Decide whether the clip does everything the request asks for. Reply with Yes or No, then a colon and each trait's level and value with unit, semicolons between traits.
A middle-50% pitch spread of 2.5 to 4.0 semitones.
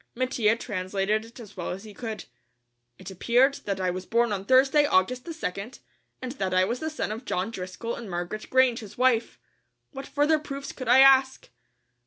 No: average, 5.1 semitones